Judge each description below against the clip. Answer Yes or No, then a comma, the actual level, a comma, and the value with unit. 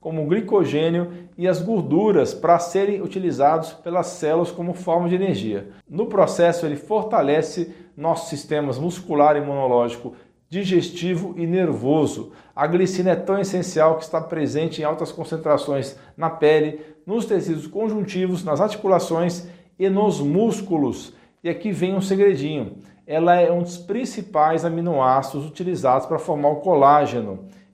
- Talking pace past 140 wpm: No, average, 135 wpm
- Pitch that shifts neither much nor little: Yes, average, 3.4 semitones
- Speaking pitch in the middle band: Yes, medium, 170 Hz